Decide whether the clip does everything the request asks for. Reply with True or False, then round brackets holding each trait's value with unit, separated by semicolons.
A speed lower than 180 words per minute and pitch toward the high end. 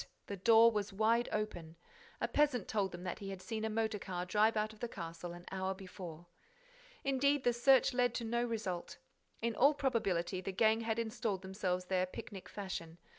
False (190 wpm; 210 Hz)